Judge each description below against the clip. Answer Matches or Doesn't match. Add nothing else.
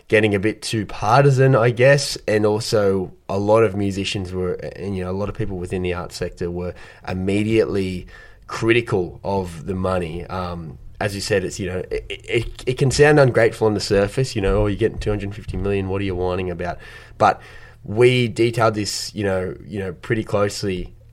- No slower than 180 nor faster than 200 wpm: Matches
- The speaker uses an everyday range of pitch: Matches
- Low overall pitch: Matches